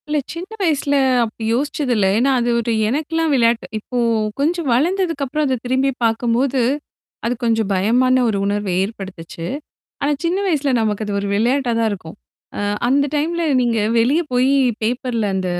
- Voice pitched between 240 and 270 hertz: Yes, very high, 250 Hz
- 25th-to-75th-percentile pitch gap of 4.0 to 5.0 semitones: Yes, average, 4.6 semitones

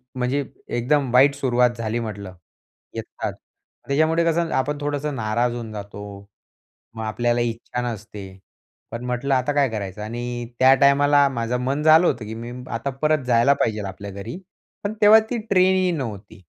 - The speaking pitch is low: Yes, low, 125 Hz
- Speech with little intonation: No, average, 4.2 semitones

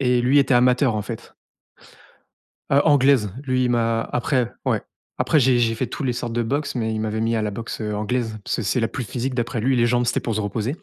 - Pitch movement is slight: Yes, narrow, 2.3 semitones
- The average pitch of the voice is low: Yes, low, 120 Hz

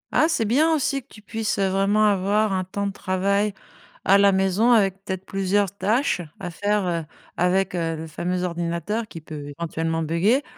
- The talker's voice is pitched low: No, high, 195 Hz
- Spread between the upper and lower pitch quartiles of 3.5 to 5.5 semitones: No, average, 3.1 semitones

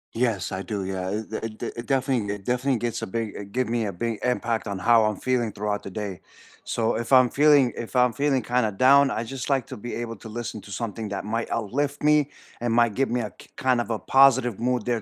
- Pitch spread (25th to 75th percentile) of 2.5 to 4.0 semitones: Yes, average, 3.1 semitones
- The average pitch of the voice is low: Yes, low, 115 Hz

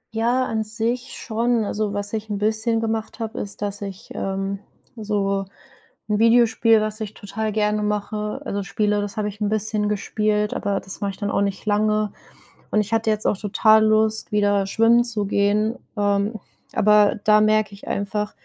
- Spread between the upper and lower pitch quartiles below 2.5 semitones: Yes, narrow, 1.3 semitones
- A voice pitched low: No, high, 210 Hz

